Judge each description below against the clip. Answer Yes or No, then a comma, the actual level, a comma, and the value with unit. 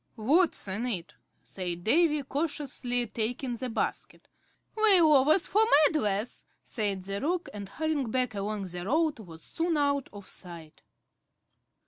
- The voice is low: No, high, 245 Hz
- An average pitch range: No, wide, 7.3 semitones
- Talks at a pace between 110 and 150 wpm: Yes, slow, 135 wpm